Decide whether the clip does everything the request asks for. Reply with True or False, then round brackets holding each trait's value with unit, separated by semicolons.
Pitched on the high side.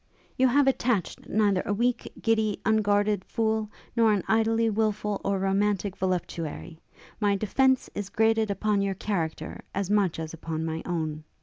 True (205 Hz)